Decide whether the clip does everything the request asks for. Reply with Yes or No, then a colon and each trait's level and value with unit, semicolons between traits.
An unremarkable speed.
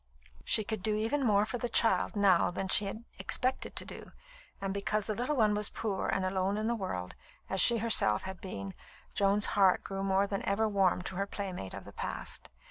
No: fast, 210 wpm